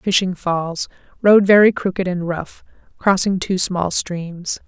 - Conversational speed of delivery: No, slow, 130 wpm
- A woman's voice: Yes, female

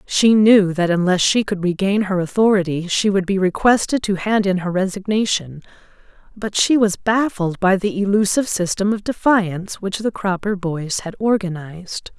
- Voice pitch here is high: Yes, high, 195 Hz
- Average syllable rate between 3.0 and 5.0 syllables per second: Yes, 4.9 syllables/s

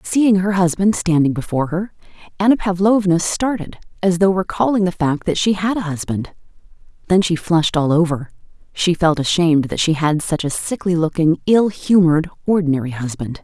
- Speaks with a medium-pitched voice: Yes, medium, 175 Hz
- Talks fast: No, average, 170 wpm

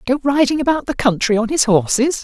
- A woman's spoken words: Yes, female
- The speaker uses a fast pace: Yes, fast, 215 wpm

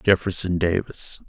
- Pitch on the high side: No, very low, 95 Hz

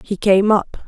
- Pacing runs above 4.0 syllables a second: No, 3.9 syllables/s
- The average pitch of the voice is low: No, high, 200 Hz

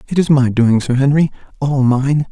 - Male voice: Yes, male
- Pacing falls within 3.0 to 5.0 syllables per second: Yes, 4.9 syllables/s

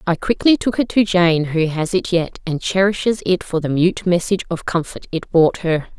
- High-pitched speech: No, medium, 180 Hz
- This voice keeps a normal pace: No, fast, 220 wpm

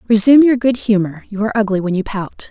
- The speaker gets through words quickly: Yes, fast, 215 wpm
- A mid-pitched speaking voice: No, high, 215 Hz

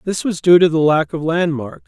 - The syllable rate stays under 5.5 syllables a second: Yes, 5.2 syllables/s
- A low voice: No, medium, 165 Hz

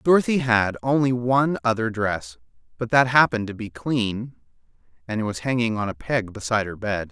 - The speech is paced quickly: No, average, 175 wpm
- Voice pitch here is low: Yes, low, 115 Hz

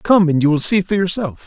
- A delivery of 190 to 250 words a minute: No, fast, 285 wpm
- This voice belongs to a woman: No, male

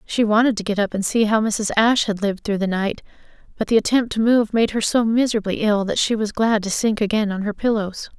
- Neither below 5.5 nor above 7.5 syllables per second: Yes, 5.9 syllables/s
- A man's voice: No, female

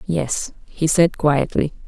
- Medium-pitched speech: Yes, medium, 155 Hz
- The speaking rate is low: Yes, slow, 130 wpm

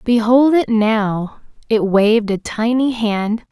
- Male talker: No, female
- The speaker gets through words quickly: No, slow, 135 wpm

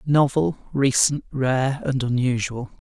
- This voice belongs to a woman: No, male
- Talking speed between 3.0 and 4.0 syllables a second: Yes, 3.8 syllables/s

